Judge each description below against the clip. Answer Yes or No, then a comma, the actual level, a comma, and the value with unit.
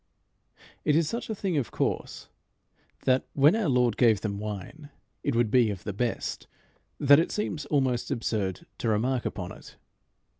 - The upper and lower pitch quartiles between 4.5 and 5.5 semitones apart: Yes, average, 5.1 semitones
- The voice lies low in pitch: Yes, low, 125 Hz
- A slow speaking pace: No, average, 175 wpm